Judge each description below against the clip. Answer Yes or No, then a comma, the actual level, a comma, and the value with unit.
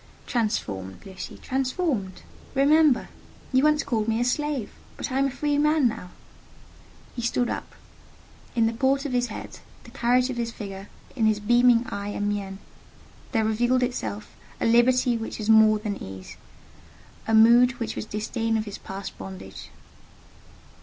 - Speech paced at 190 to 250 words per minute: No, average, 160 wpm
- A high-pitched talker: Yes, high, 230 Hz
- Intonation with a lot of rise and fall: No, average, 3.6 semitones